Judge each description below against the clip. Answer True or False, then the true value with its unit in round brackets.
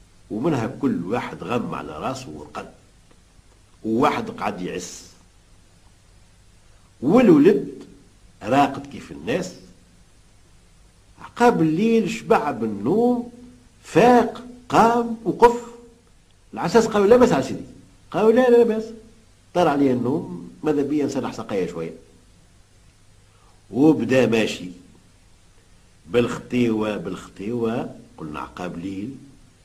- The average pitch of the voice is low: True (105 Hz)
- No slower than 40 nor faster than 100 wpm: True (95 wpm)